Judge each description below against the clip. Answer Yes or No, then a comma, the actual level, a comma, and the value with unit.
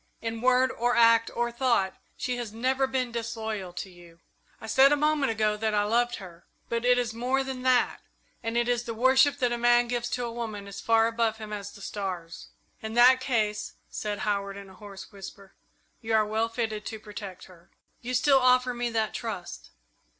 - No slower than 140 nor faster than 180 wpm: No, average, 200 wpm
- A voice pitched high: Yes, high, 230 Hz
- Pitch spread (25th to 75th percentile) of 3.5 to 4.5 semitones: No, average, 2.8 semitones